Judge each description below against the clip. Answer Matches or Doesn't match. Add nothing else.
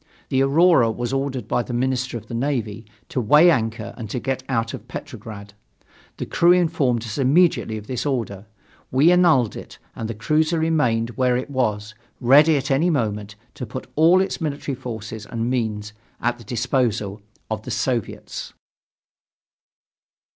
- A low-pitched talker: Matches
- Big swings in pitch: Doesn't match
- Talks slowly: Doesn't match